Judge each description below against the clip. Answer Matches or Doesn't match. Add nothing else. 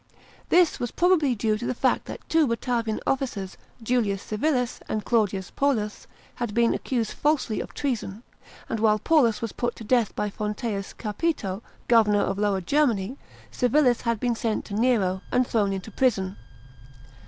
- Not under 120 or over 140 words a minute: Doesn't match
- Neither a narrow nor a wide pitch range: Matches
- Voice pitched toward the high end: Matches